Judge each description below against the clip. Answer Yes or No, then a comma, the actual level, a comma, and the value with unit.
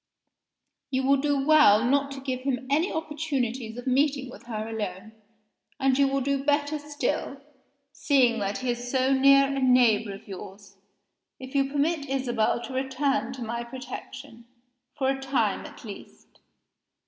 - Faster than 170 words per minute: No, average, 160 wpm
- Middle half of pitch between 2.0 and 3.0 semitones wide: Yes, average, 2.7 semitones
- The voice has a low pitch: No, very high, 265 Hz